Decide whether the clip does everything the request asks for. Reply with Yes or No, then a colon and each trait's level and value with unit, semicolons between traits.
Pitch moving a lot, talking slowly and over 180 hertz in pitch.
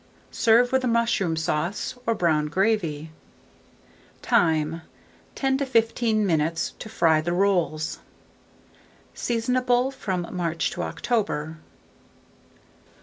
Yes: wide, 6.4 semitones; slow, 95 wpm; high, 190 Hz